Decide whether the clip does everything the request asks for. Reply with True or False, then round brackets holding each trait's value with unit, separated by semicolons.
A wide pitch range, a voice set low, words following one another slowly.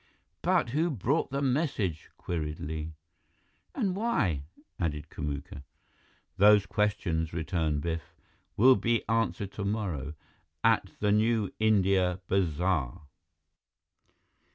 True (5.9 semitones; 95 Hz; 100 wpm)